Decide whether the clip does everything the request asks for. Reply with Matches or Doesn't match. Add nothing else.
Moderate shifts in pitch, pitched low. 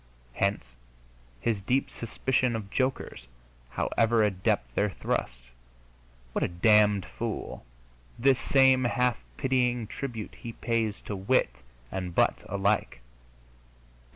Matches